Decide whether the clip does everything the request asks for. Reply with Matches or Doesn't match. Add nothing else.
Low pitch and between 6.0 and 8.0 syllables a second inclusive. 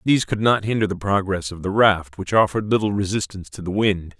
Matches